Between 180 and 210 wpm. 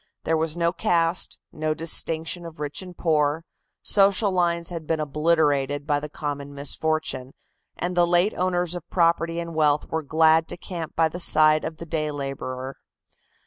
No: average, 170 wpm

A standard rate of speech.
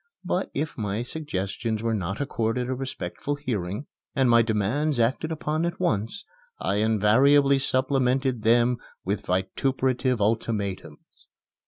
No: slow, 125 wpm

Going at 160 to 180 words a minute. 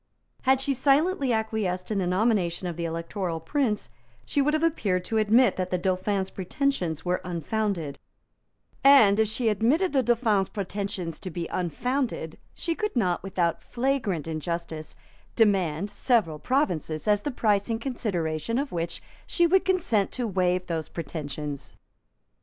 No: average, 150 wpm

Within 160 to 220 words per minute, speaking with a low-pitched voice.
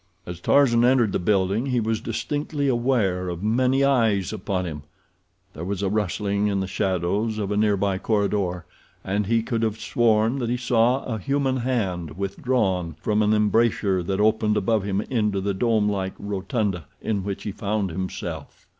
Yes: average, 170 wpm; low, 105 Hz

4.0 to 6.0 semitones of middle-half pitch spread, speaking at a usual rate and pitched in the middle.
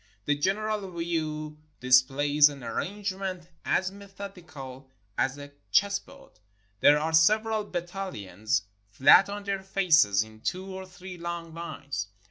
No: wide, 5.4 semitones; slow, 125 wpm; medium, 170 Hz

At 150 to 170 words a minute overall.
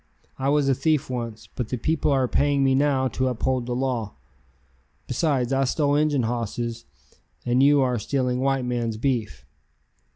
Yes: average, 165 wpm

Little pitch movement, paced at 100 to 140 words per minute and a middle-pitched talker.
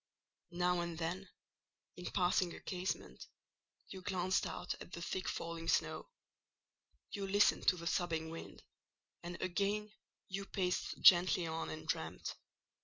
Yes: narrow, 1.7 semitones; slow, 135 wpm; medium, 180 Hz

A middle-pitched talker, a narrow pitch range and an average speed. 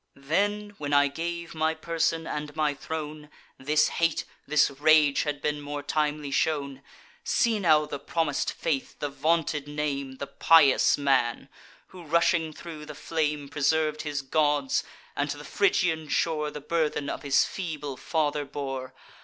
Yes: medium, 150 Hz; narrow, 2.0 semitones; average, 155 wpm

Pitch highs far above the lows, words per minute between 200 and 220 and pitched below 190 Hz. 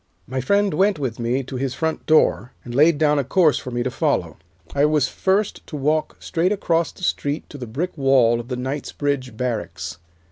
No: average, 4.2 semitones; fast, 205 wpm; medium, 140 Hz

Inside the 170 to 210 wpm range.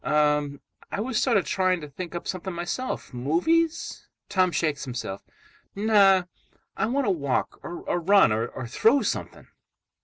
No: average, 150 wpm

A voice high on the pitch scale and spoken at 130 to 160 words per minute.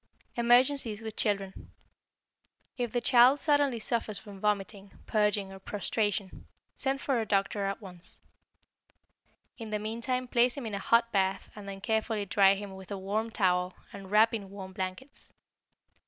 Yes: high, 210 Hz; average, 155 wpm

